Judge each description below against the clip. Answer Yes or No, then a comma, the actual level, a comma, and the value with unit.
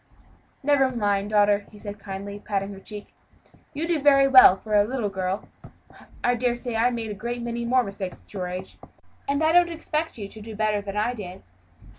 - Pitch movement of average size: Yes, average, 3.9 semitones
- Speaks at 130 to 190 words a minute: No, fast, 205 wpm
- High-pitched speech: Yes, high, 215 Hz